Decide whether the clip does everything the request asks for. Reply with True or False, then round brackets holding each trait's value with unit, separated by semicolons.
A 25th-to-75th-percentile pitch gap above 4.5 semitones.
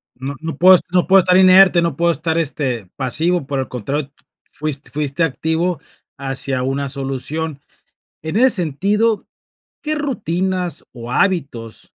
True (5.0 semitones)